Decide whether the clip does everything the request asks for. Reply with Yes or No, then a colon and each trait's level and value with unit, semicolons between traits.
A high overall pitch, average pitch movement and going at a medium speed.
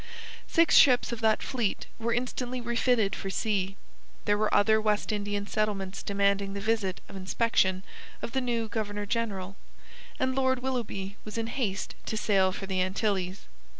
Yes: high, 210 Hz; average, 3.0 semitones; average, 160 wpm